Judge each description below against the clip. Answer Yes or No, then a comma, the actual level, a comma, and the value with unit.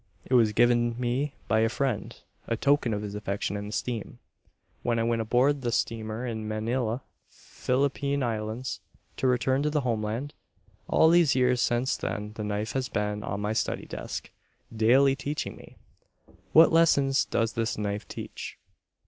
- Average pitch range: Yes, average, 3.6 semitones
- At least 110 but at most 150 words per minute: No, average, 160 wpm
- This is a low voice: Yes, low, 120 Hz